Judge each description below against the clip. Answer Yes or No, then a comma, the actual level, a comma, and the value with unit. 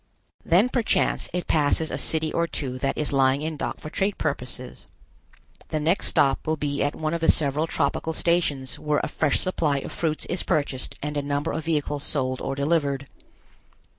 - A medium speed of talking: Yes, average, 190 wpm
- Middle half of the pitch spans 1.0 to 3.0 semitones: Yes, narrow, 2.5 semitones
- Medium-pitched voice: Yes, medium, 150 Hz